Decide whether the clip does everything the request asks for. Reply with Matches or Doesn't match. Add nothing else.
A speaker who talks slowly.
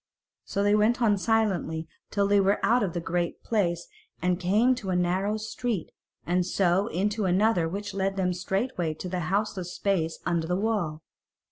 Doesn't match